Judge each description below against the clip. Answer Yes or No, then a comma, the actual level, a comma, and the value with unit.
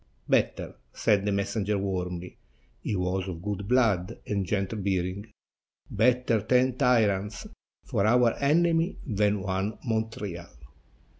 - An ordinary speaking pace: No, slow, 120 wpm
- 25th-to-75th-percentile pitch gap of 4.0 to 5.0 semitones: No, average, 3.2 semitones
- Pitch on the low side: Yes, low, 105 Hz